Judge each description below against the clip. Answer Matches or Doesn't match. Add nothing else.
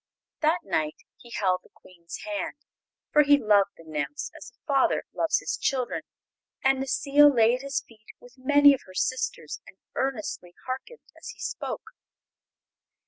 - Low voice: Doesn't match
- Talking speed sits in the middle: Matches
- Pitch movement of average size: Doesn't match